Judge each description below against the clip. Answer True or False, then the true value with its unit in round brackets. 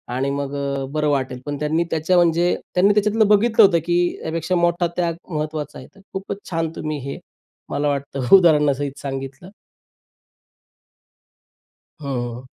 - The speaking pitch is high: False (155 Hz)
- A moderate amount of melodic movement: True (4.0 semitones)